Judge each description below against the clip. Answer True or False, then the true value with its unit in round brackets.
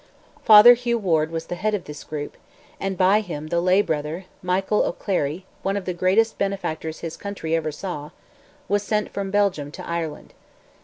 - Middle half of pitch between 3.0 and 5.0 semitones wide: True (4.0 semitones)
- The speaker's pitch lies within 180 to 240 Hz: True (185 Hz)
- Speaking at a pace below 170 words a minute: False (175 wpm)